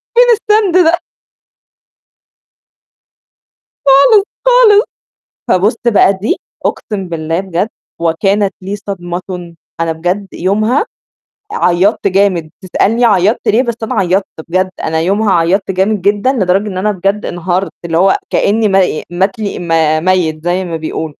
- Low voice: No, high, 190 Hz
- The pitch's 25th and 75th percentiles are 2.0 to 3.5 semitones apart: Yes, average, 3.1 semitones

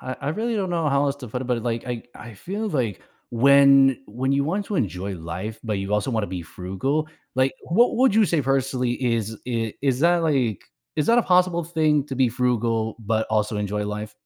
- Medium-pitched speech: No, low, 125 Hz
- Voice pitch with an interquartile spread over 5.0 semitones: Yes, wide, 5.6 semitones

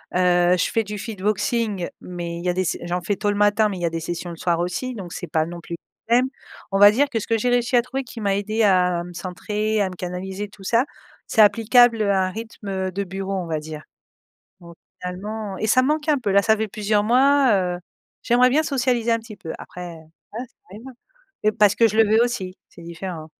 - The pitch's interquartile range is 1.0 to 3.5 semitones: No, average, 4.1 semitones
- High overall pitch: Yes, high, 205 Hz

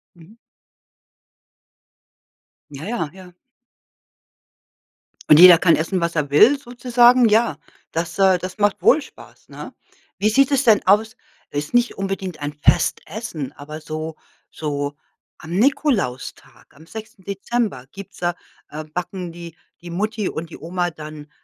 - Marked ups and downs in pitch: Yes, wide, 5.7 semitones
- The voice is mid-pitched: Yes, medium, 180 Hz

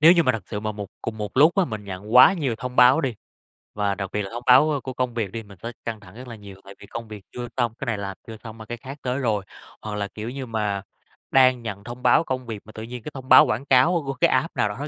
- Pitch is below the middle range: Yes, low, 115 Hz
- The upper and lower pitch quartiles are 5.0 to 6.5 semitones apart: No, average, 3.7 semitones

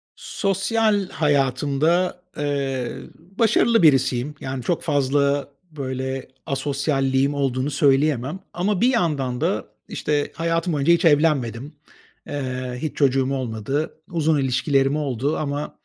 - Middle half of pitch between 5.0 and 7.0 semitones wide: No, average, 3.0 semitones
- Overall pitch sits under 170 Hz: Yes, medium, 140 Hz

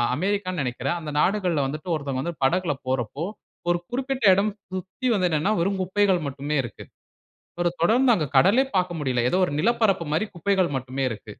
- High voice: No, medium, 175 Hz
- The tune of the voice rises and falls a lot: Yes, wide, 5.7 semitones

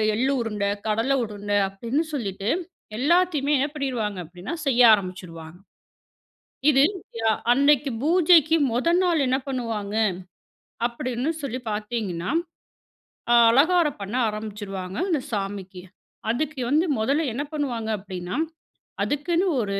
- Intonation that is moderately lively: No, wide, 6.1 semitones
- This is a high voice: Yes, high, 235 Hz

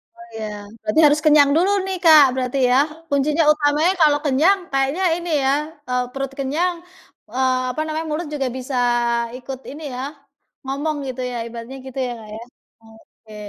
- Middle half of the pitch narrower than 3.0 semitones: No, average, 3.3 semitones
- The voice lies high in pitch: Yes, very high, 275 Hz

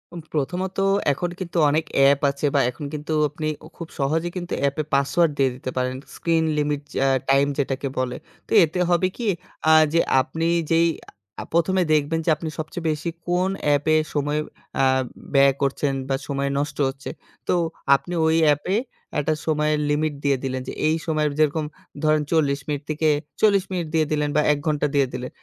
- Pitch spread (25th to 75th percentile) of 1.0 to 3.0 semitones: Yes, average, 2.7 semitones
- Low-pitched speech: No, medium, 150 Hz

